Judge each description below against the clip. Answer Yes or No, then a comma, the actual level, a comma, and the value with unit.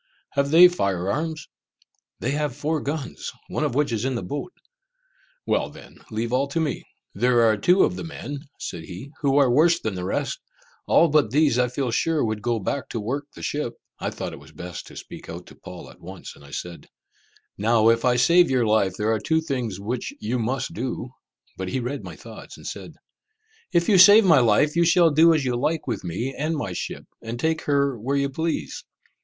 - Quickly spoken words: Yes, fast, 220 wpm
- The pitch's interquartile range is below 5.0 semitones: No, average, 5.3 semitones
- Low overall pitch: Yes, low, 130 Hz